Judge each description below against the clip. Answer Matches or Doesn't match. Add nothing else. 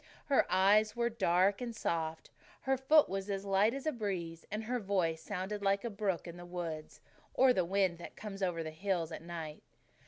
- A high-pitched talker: Matches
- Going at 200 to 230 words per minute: Matches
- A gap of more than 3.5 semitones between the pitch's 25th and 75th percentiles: Matches